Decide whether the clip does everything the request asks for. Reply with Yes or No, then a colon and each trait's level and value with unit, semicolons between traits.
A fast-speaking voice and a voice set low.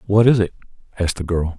Yes: fast, 225 wpm; very low, 95 Hz